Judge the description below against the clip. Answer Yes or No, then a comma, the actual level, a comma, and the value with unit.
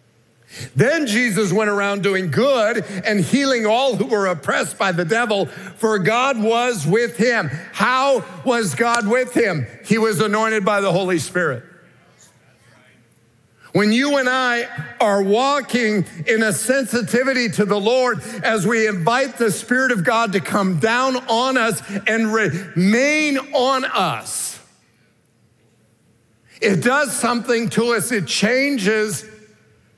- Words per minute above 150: No, slow, 135 wpm